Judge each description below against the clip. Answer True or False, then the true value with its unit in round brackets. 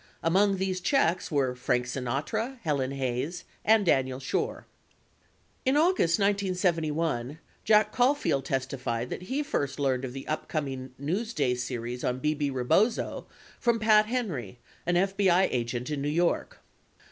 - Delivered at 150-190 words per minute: False (135 wpm)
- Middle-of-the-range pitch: True (155 Hz)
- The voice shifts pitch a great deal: True (7.3 semitones)